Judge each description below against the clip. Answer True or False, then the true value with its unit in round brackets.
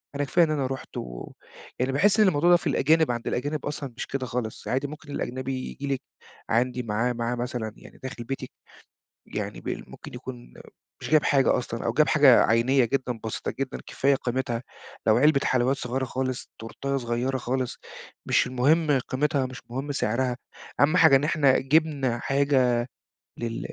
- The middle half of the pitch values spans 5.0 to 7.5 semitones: False (2.8 semitones)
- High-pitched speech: False (130 Hz)